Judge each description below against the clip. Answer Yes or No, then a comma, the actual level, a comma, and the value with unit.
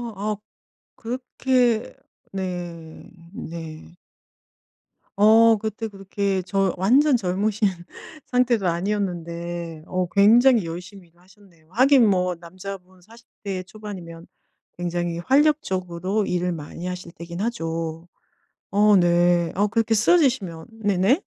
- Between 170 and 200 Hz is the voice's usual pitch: Yes, high, 190 Hz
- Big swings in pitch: No, average, 3.9 semitones